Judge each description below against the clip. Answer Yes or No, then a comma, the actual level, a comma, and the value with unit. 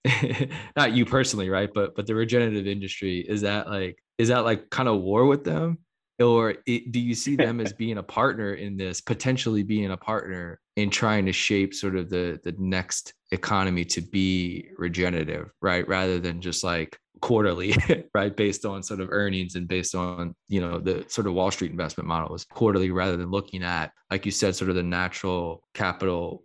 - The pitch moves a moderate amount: Yes, average, 3.4 semitones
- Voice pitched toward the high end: No, low, 100 Hz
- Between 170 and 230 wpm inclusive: Yes, average, 195 wpm